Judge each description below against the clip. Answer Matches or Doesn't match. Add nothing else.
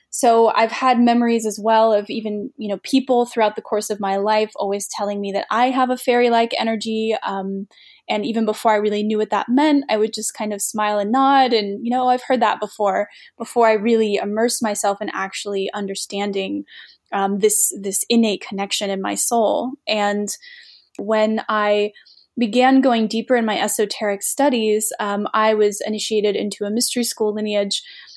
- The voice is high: Matches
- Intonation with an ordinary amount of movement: Doesn't match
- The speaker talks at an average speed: Matches